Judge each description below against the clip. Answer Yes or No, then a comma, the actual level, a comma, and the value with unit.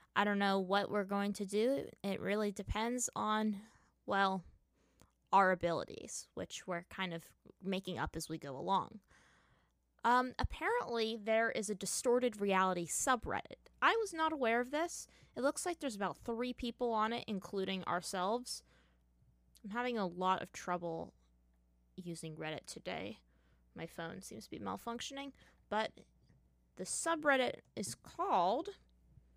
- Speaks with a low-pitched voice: No, high, 200 Hz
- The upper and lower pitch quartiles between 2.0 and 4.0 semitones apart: No, wide, 5.5 semitones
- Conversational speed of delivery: Yes, average, 145 wpm